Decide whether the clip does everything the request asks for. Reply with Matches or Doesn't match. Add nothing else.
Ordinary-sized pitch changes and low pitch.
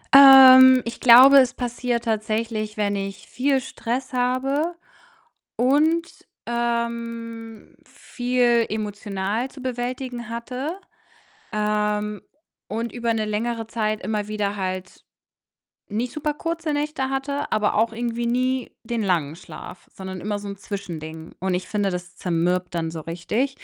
Doesn't match